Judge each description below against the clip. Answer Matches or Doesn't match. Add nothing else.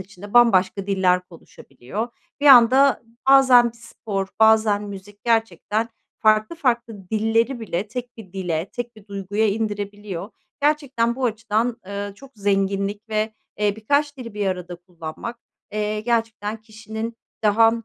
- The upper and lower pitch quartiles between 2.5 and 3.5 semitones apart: Matches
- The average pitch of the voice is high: Matches